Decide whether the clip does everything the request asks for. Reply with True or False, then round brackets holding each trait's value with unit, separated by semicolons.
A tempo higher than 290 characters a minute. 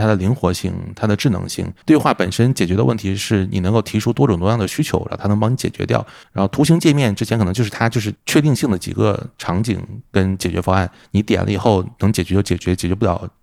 True (375 characters per minute)